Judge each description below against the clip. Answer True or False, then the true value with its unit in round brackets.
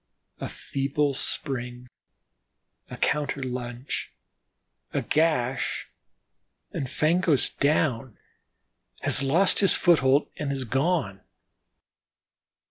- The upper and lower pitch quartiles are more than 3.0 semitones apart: True (3.5 semitones)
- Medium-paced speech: False (85 wpm)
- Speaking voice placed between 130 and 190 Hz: True (140 Hz)